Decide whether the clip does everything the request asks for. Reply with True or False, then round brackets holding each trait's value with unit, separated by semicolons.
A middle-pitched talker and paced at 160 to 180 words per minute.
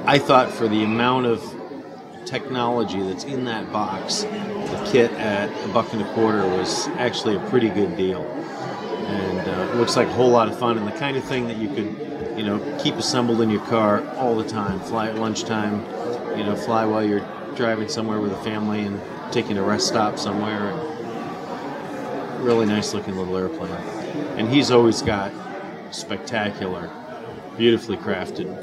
False (110 Hz; 175 wpm)